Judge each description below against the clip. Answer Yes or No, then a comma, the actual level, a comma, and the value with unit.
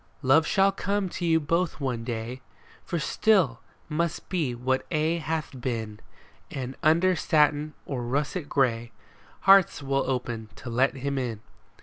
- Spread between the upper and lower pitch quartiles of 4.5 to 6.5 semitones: Yes, average, 4.8 semitones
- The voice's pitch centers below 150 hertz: Yes, medium, 140 Hz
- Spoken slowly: No, average, 145 wpm